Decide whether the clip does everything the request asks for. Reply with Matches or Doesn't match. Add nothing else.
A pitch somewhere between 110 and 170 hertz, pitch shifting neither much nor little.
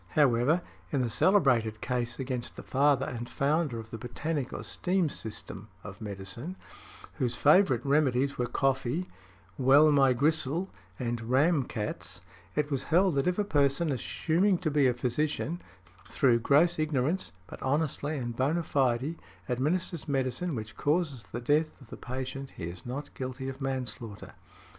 Matches